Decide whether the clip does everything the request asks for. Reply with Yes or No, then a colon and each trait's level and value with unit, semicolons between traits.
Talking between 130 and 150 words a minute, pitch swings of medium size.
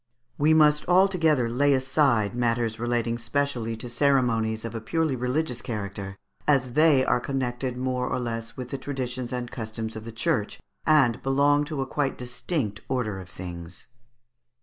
No: average, 160 wpm; average, 3.7 semitones